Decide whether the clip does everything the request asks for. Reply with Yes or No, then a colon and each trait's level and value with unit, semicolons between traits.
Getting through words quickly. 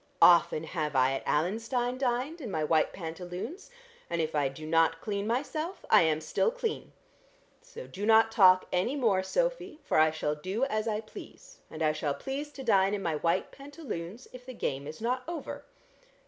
No: average, 190 wpm